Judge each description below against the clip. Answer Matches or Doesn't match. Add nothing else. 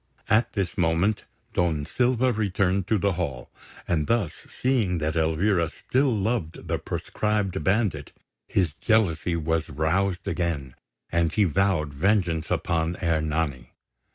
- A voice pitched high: Doesn't match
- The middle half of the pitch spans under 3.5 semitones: Doesn't match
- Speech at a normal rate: Doesn't match